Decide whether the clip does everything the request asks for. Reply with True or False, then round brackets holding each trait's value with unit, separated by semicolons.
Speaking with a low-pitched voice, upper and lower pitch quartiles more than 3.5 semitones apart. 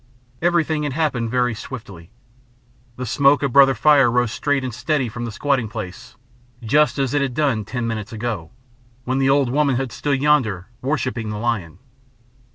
True (125 Hz; 3.9 semitones)